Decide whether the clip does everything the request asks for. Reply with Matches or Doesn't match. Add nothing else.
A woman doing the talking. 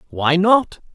Doesn't match